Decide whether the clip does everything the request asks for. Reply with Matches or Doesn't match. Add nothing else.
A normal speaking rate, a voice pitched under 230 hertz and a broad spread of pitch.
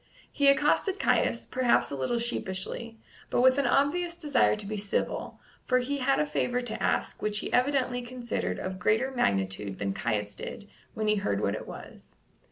Doesn't match